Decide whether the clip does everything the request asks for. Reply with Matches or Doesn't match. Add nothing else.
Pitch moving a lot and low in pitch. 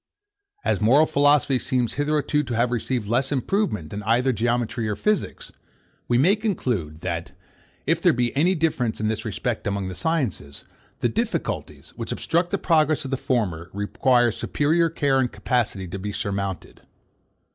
Matches